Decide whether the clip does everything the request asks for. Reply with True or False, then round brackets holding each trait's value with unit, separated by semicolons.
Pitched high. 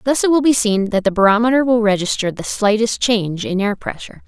True (215 Hz)